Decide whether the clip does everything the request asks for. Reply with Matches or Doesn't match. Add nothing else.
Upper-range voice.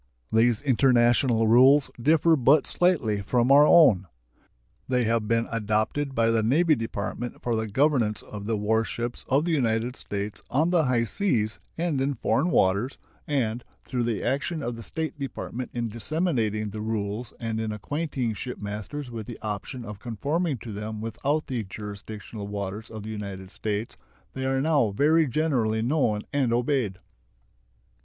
Doesn't match